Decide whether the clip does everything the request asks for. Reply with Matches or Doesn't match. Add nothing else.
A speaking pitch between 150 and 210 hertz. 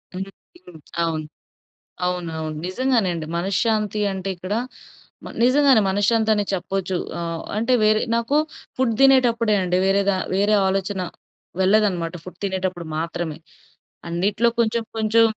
Matches